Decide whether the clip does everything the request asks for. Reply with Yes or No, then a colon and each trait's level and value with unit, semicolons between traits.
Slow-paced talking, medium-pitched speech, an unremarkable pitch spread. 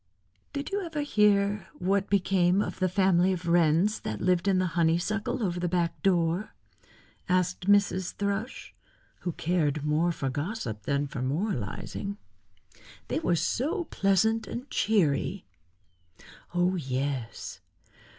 Yes: slow, 125 wpm; medium, 180 Hz; average, 3.4 semitones